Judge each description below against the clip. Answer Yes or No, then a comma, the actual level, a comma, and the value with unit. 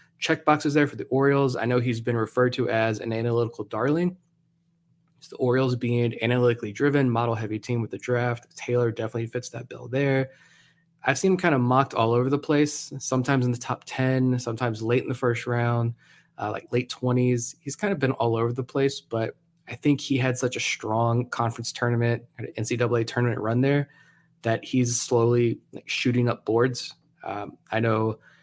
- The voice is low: Yes, low, 125 Hz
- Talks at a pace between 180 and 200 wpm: Yes, average, 195 wpm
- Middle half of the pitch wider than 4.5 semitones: No, average, 2.9 semitones